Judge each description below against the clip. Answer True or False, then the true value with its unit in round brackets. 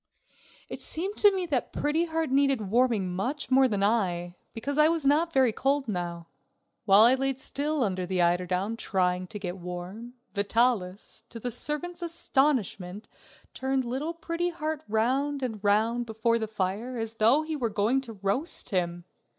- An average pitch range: False (6.2 semitones)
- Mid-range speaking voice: False (235 Hz)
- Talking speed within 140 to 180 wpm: True (165 wpm)